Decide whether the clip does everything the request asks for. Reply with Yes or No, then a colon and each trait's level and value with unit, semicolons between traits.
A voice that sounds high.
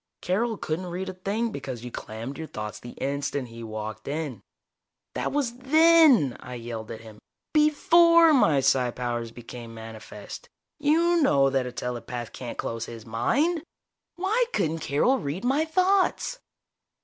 No: medium, 140 Hz